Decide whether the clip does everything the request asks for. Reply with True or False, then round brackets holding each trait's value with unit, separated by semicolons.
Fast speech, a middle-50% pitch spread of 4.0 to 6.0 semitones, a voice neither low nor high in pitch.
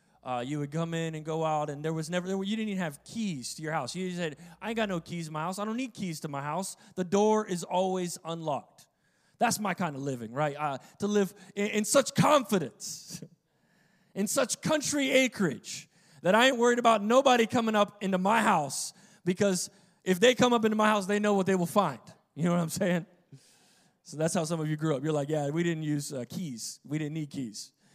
True (235 wpm; 4.6 semitones; 180 Hz)